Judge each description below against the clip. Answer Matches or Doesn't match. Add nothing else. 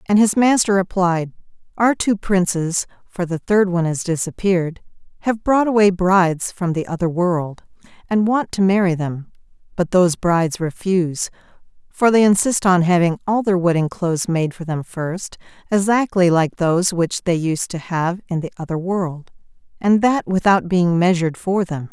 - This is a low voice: Doesn't match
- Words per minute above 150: Matches